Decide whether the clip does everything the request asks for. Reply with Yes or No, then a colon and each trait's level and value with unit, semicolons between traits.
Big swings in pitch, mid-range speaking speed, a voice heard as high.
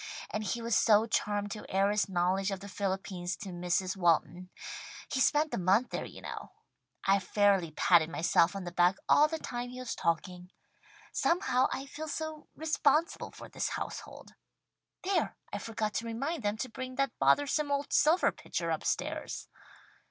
Yes: wide, 6.7 semitones; average, 170 wpm; high, 210 Hz